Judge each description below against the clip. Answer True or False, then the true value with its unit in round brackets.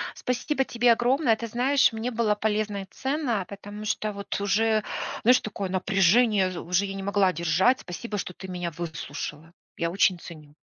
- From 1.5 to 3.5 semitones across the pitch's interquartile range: False (4.2 semitones)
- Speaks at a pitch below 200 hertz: False (205 Hz)